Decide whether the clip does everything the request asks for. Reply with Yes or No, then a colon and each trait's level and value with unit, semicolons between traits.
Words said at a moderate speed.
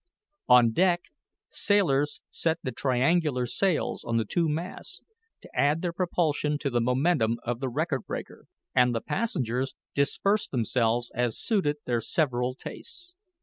Yes: average, 145 wpm